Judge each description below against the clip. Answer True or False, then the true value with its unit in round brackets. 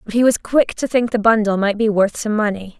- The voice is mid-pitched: False (215 Hz)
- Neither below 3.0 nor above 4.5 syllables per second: False (5.6 syllables/s)